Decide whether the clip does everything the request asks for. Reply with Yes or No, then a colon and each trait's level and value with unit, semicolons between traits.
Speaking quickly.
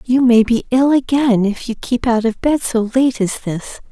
Yes: fast, 230 wpm